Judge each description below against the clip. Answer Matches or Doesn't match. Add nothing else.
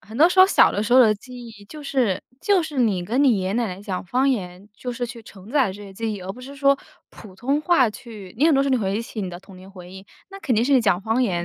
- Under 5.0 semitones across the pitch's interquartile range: Doesn't match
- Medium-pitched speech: Doesn't match